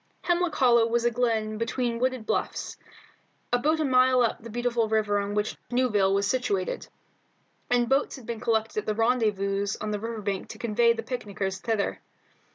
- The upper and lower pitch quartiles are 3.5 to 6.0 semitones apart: No, average, 2.7 semitones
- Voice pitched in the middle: No, high, 230 Hz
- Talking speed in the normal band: Yes, average, 175 wpm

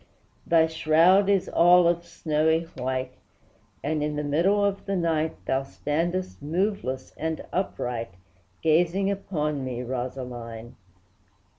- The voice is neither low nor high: Yes, medium, 160 Hz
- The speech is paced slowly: Yes, slow, 120 wpm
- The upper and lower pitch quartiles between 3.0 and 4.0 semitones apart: No, average, 5.0 semitones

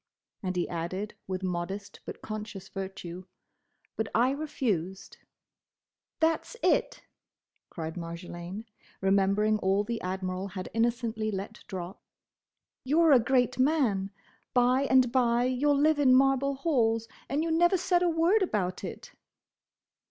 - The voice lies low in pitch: No, high, 225 Hz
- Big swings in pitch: Yes, wide, 6.1 semitones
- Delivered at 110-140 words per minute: Yes, slow, 135 wpm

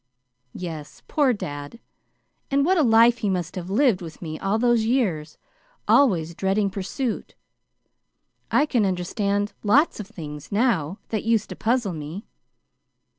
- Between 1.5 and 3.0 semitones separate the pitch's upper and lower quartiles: No, average, 5.3 semitones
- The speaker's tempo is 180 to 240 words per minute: No, average, 140 wpm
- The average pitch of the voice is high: Yes, high, 205 Hz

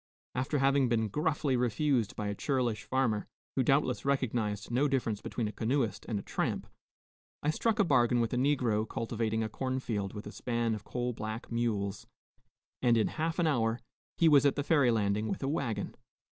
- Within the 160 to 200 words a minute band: Yes, average, 185 wpm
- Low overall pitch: Yes, low, 120 Hz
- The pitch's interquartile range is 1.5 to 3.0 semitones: No, average, 3.9 semitones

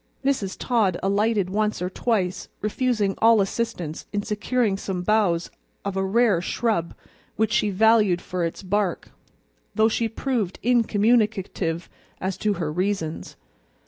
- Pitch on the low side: No, high, 205 Hz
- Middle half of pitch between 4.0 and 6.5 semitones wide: No, average, 3.3 semitones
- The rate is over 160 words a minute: No, slow, 135 wpm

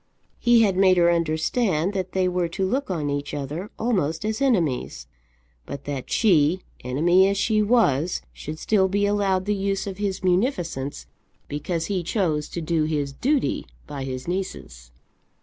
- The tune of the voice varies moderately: Yes, average, 4.8 semitones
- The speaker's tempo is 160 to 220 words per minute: Yes, average, 165 wpm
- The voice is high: No, medium, 180 Hz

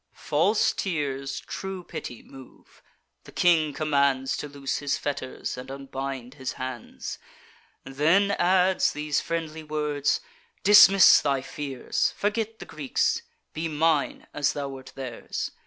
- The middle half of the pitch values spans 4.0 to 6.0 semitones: No, average, 3.4 semitones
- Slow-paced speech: Yes, slow, 125 wpm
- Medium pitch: Yes, medium, 145 Hz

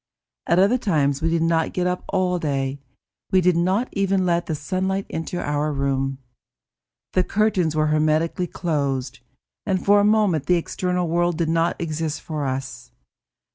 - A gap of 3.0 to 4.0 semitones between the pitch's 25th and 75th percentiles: Yes, average, 3.4 semitones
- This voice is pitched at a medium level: Yes, medium, 170 Hz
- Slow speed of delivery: No, average, 165 wpm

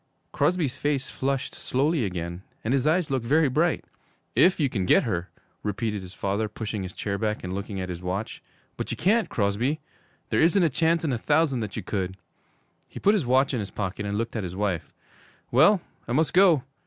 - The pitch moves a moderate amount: No, wide, 7.3 semitones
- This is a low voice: Yes, low, 120 Hz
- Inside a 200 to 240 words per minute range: Yes, fast, 205 wpm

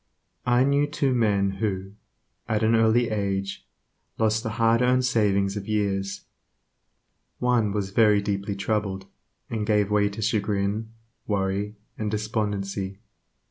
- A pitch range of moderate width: No, narrow, 2.3 semitones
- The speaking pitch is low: Yes, low, 105 Hz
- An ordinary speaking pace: No, slow, 130 wpm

